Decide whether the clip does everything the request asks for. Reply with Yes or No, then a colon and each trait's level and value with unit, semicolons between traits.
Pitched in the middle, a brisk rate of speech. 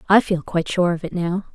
Yes: medium, 180 Hz; fast, 270 wpm